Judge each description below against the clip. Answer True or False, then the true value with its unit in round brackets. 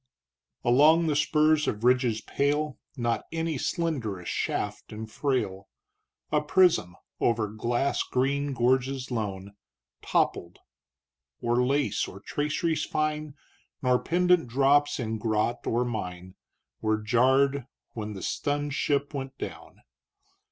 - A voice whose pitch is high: False (130 Hz)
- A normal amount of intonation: True (4.7 semitones)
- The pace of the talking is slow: True (115 wpm)